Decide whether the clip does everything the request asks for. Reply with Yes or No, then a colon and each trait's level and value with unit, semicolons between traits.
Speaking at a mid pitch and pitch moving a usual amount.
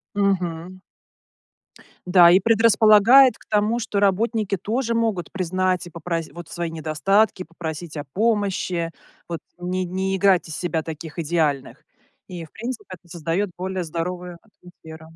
Yes: medium, 180 Hz; average, 3.5 semitones